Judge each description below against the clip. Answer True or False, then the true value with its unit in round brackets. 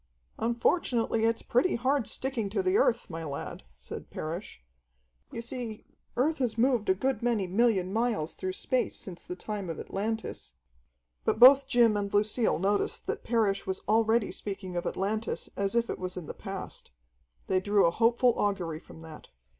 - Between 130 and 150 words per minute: False (170 wpm)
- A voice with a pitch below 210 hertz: False (215 Hz)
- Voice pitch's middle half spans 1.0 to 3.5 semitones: False (4.1 semitones)